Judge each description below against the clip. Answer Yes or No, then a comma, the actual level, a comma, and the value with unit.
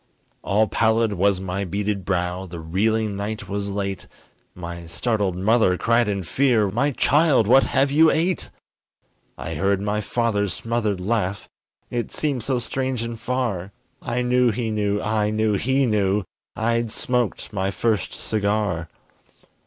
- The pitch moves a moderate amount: Yes, average, 3.2 semitones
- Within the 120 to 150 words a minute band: Yes, average, 145 wpm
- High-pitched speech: No, low, 105 Hz